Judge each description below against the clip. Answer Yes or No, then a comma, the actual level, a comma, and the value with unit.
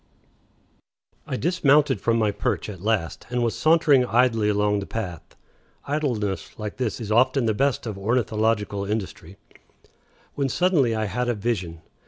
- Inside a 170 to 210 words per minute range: No, average, 150 wpm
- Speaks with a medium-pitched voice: No, low, 115 Hz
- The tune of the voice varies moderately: Yes, average, 3.8 semitones